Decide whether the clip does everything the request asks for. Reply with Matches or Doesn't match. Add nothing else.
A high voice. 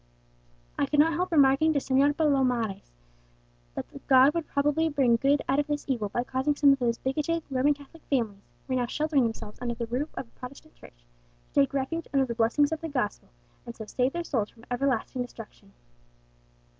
Matches